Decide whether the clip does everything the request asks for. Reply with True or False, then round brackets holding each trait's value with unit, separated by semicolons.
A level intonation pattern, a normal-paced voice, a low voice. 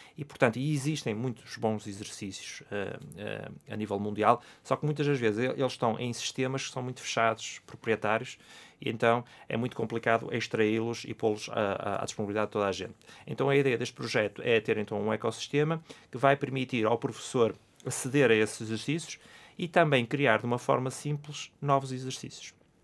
False (3.7 semitones; 175 wpm; 120 Hz)